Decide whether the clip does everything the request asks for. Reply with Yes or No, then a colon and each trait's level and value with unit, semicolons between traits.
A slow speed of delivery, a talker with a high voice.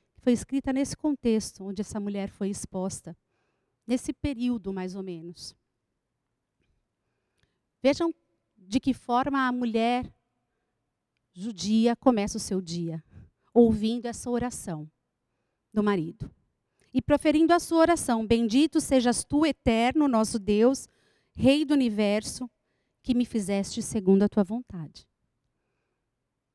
Yes: slow, 115 wpm; high, 230 Hz